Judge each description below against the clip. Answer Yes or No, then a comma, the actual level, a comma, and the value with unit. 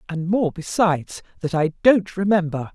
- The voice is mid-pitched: Yes, medium, 180 Hz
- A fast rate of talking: No, average, 155 wpm